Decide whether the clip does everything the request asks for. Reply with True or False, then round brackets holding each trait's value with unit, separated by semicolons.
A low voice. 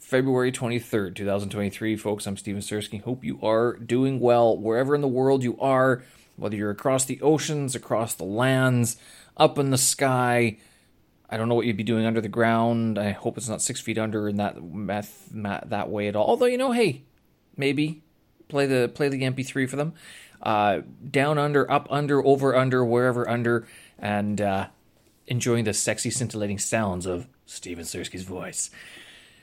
True (115 Hz)